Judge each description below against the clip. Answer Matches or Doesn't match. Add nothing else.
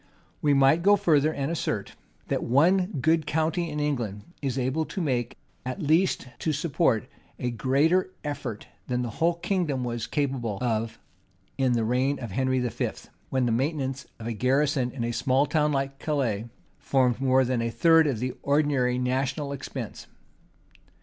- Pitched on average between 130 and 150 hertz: Matches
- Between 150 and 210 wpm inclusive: Matches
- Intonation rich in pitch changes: Doesn't match